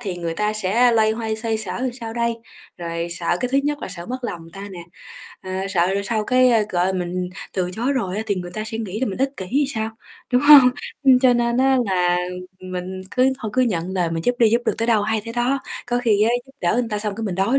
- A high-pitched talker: Yes, high, 220 Hz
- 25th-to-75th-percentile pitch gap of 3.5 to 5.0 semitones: Yes, average, 4.7 semitones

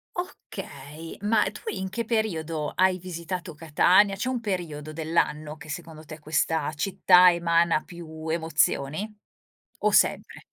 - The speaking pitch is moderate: Yes, medium, 165 Hz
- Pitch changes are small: No, average, 3.3 semitones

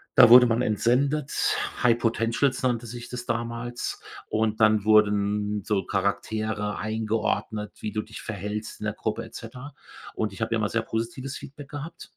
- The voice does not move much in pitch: Yes, narrow, 2.2 semitones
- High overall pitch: No, low, 110 Hz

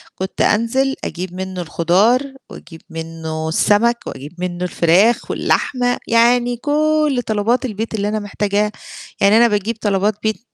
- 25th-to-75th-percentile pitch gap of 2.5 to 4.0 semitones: No, average, 4.7 semitones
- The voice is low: No, high, 210 Hz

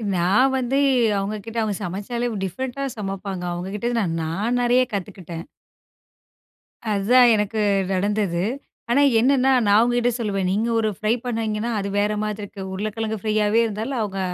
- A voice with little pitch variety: No, average, 3.3 semitones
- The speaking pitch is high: Yes, high, 215 Hz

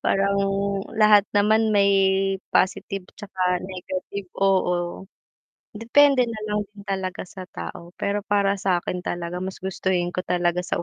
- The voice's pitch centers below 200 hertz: Yes, high, 190 Hz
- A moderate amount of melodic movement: No, narrow, 2.2 semitones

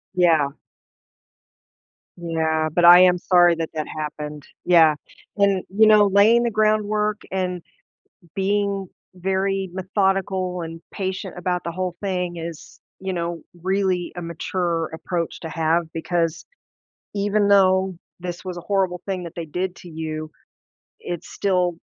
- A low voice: No, medium, 180 Hz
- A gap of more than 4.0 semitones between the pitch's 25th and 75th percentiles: No, narrow, 2.4 semitones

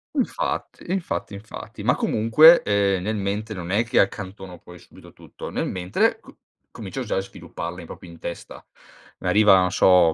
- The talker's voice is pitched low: Yes, low, 100 Hz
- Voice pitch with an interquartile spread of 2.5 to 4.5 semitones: Yes, average, 2.9 semitones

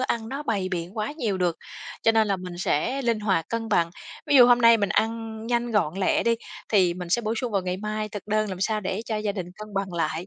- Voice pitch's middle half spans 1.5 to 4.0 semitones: Yes, average, 3.7 semitones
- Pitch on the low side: No, high, 215 Hz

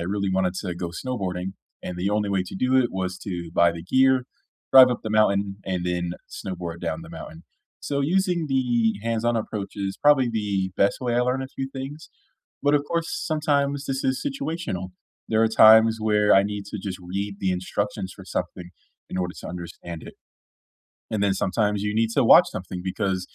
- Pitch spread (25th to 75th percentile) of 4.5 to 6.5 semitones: Yes, wide, 5.6 semitones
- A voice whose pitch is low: Yes, low, 105 Hz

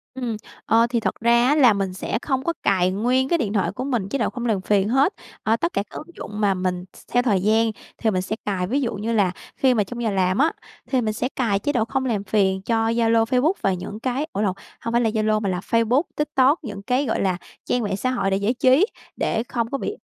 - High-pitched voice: Yes, high, 225 Hz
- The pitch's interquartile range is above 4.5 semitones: No, average, 4.2 semitones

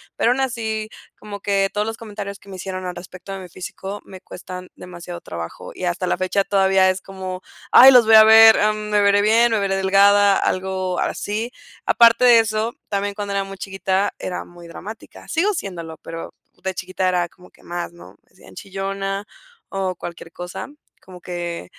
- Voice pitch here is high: Yes, high, 195 Hz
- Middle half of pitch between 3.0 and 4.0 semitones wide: No, narrow, 2.5 semitones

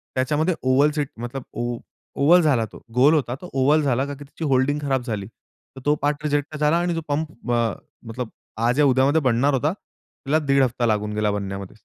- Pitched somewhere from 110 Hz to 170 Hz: Yes, low, 135 Hz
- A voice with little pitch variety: No, average, 3.5 semitones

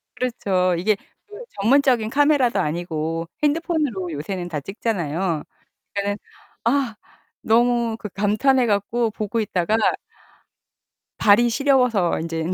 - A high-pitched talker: Yes, high, 210 Hz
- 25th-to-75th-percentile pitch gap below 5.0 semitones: No, average, 5.3 semitones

